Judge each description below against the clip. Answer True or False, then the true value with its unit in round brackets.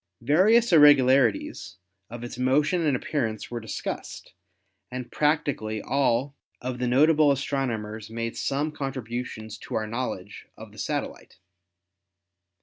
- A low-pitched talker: True (130 Hz)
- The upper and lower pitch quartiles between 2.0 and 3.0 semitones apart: False (4.0 semitones)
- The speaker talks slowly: True (120 wpm)